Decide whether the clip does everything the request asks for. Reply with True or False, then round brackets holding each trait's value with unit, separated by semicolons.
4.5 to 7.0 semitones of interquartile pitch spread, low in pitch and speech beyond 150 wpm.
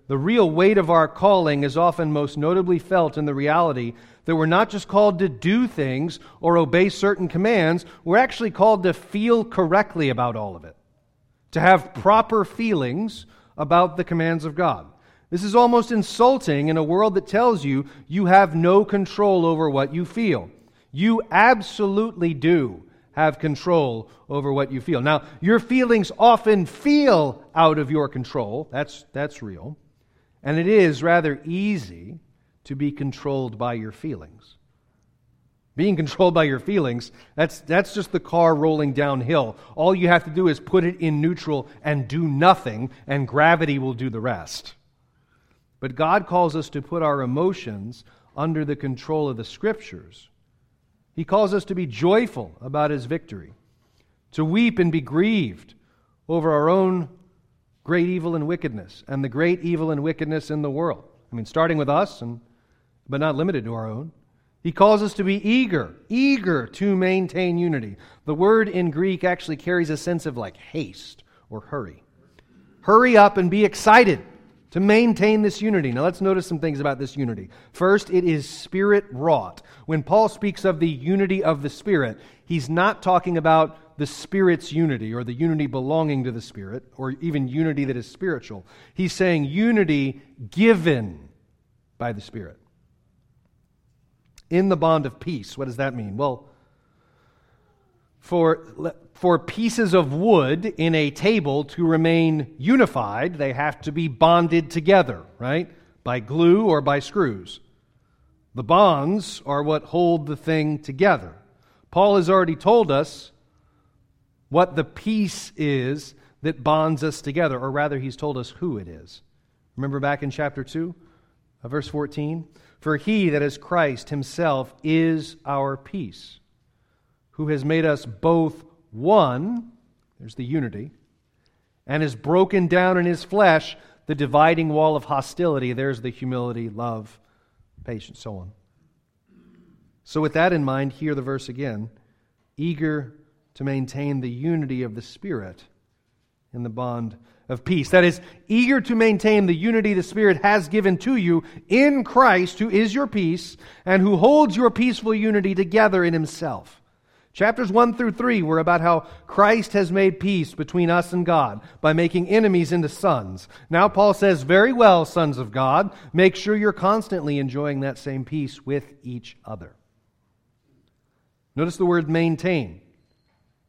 False (5.2 semitones; 160 Hz; 160 wpm)